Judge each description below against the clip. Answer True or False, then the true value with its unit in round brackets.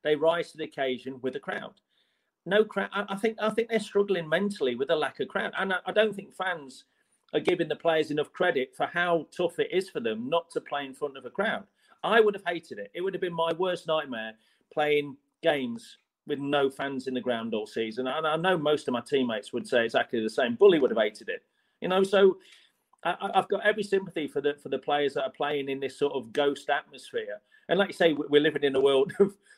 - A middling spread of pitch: False (5.8 semitones)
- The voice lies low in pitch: False (165 Hz)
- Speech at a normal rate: False (255 wpm)